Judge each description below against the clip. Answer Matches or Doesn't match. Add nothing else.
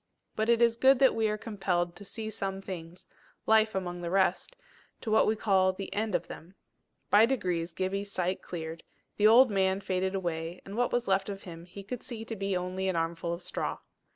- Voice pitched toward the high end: Matches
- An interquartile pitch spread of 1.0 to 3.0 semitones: Doesn't match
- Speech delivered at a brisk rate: Matches